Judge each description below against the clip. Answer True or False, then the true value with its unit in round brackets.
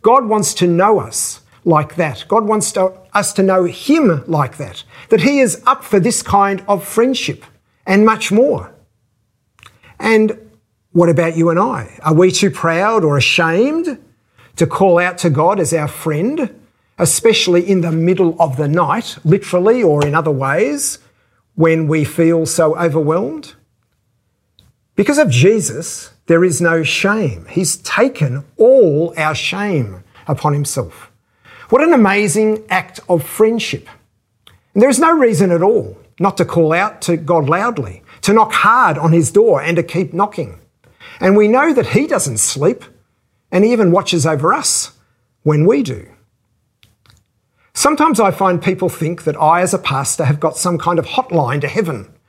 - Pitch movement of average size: False (5.7 semitones)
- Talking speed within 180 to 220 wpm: False (165 wpm)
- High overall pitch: False (170 Hz)